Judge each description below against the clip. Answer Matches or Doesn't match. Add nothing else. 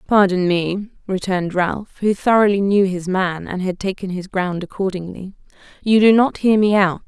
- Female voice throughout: Matches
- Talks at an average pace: Matches